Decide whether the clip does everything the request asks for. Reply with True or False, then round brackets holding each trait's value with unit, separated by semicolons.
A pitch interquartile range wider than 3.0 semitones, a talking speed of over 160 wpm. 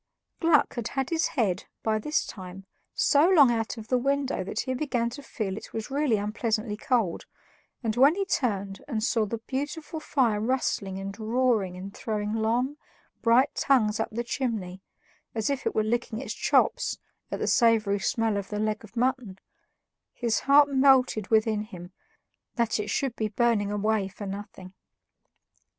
True (3.9 semitones; 170 wpm)